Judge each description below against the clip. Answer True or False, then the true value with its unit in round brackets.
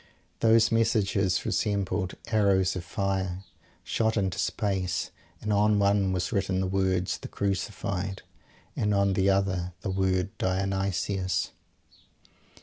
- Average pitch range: False (1.3 semitones)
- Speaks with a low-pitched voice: True (95 Hz)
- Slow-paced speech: True (120 wpm)